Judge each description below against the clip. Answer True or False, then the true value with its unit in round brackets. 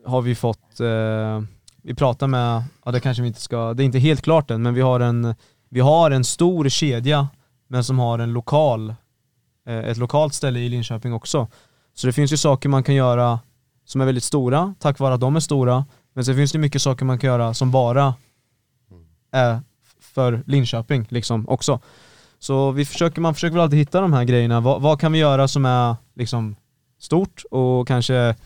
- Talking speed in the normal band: False (200 wpm)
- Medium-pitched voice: False (130 Hz)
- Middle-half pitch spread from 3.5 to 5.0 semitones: False (2.8 semitones)